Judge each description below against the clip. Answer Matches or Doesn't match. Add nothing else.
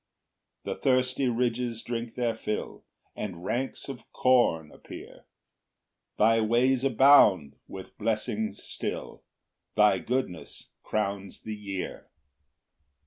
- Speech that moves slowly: Matches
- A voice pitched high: Doesn't match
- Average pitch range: Matches